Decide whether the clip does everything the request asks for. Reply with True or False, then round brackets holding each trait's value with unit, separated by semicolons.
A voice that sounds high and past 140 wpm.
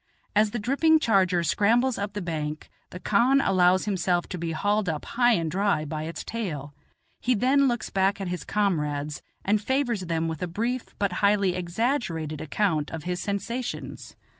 True (195 Hz; 175 wpm)